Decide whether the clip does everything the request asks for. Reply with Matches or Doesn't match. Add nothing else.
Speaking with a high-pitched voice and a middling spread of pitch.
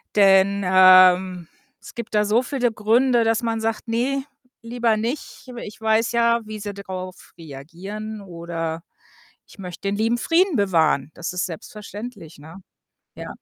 Matches